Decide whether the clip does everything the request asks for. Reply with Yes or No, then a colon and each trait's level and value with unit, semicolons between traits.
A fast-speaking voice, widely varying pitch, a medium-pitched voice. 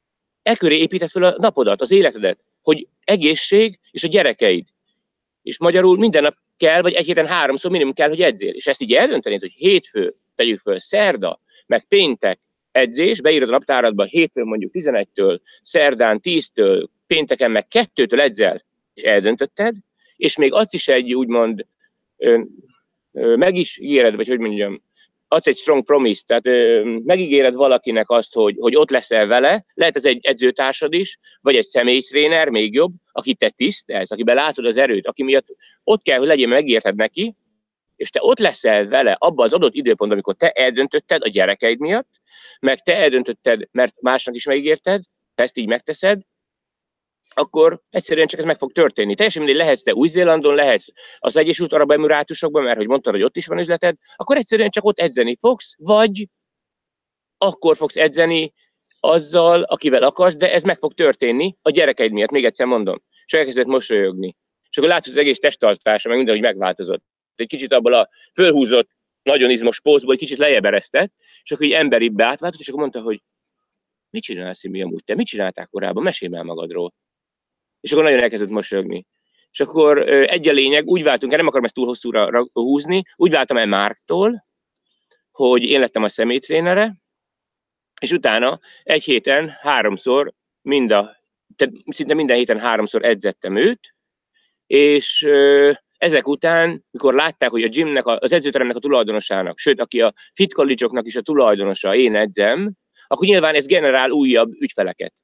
Yes: fast, 165 wpm; wide, 8.9 semitones; medium, 170 Hz